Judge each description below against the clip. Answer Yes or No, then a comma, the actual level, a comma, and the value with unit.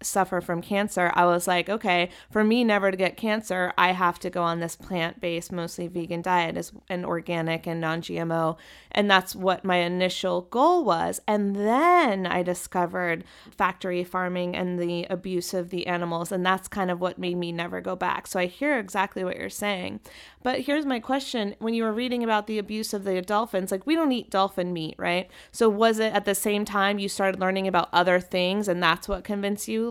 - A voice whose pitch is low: No, medium, 185 Hz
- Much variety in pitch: No, average, 3.0 semitones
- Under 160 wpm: No, fast, 205 wpm